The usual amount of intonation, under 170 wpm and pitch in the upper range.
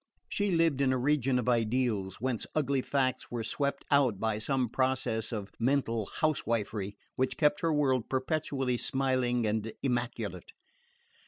No: average, 3.4 semitones; average, 145 wpm; low, 130 Hz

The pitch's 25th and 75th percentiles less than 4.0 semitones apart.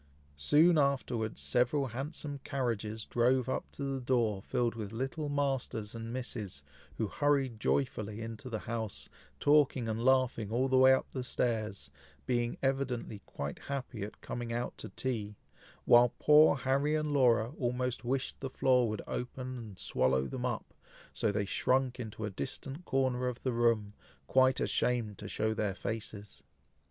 Yes: average, 3.3 semitones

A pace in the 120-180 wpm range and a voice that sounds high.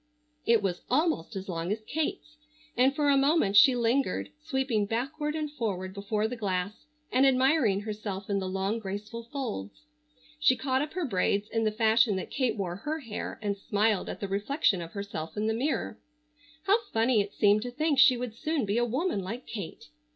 No: average, 195 wpm; high, 225 Hz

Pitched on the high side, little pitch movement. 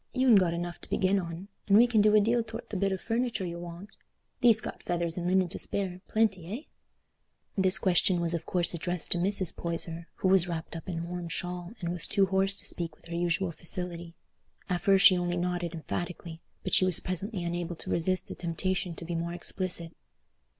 No: medium, 180 Hz; narrow, 2.1 semitones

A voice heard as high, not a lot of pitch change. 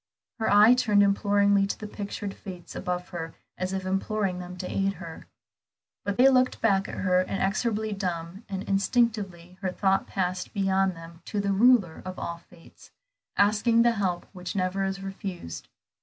Yes: high, 195 Hz; narrow, 2.1 semitones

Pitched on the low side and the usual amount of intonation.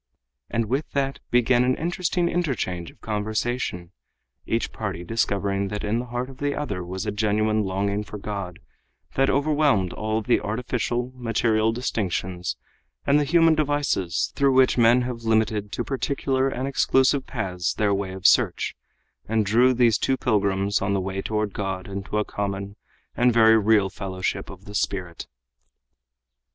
Yes: low, 110 Hz; average, 4.5 semitones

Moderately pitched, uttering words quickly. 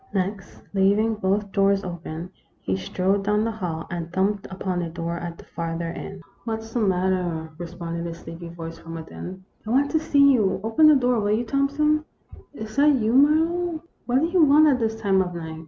No: high, 195 Hz; fast, 220 wpm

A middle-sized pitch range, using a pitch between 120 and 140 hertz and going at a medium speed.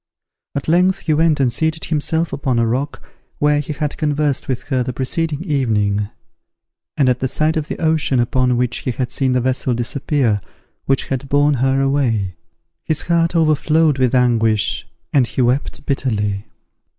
Yes: average, 3.6 semitones; low, 135 Hz; average, 170 wpm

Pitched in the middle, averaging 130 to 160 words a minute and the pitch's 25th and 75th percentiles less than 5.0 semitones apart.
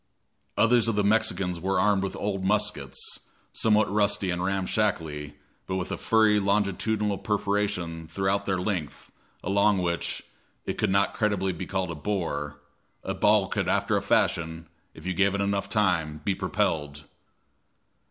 No: very low, 95 Hz; average, 150 wpm; average, 3.2 semitones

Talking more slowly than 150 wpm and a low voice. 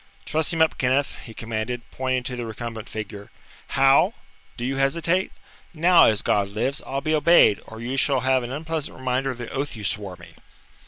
No: average, 195 wpm; low, 130 Hz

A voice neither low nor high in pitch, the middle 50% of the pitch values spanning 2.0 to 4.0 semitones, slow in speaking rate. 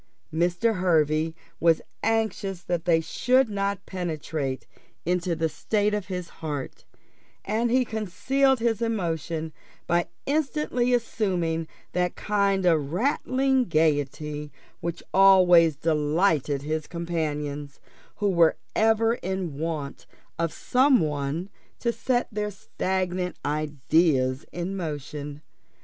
No: medium, 175 Hz; average, 5.1 semitones; slow, 110 wpm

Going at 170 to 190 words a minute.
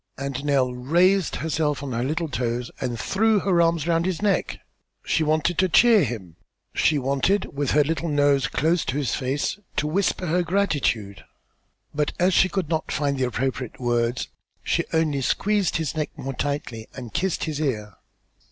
Yes: average, 175 wpm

